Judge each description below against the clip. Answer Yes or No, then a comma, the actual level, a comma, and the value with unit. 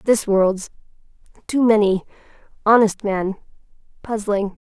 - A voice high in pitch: Yes, high, 210 Hz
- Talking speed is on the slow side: Yes, slow, 50 wpm